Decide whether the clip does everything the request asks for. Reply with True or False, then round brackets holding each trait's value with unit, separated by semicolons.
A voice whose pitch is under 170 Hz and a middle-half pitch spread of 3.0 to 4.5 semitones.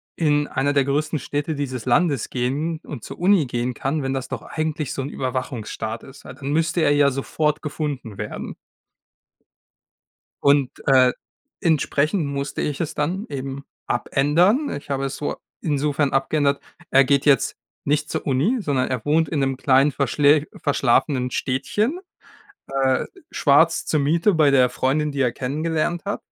False (140 Hz; 2.5 semitones)